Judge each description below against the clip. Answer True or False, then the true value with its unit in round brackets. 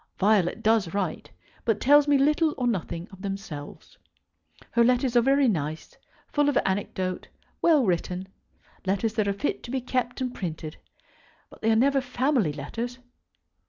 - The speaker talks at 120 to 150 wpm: False (160 wpm)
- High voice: True (225 Hz)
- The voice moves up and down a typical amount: False (5.7 semitones)